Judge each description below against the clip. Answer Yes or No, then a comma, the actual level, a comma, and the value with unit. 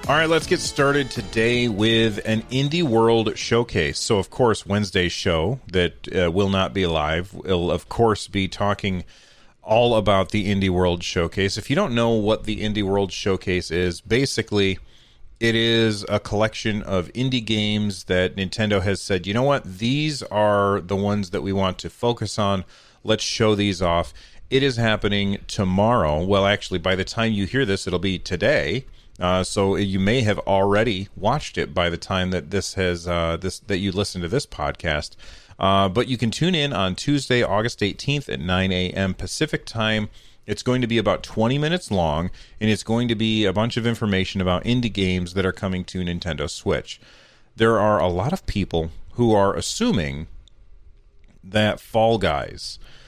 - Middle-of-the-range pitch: No, low, 100 Hz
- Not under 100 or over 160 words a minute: No, average, 185 wpm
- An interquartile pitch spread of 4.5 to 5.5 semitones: No, average, 3.5 semitones